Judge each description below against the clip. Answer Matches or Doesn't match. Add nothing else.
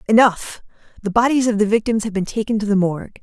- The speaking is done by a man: Doesn't match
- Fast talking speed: Matches